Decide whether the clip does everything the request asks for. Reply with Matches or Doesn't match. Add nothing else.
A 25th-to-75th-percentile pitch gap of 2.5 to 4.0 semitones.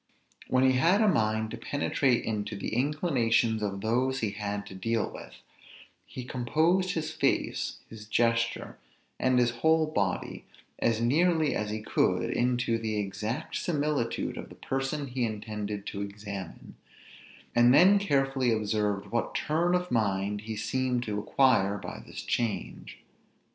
Doesn't match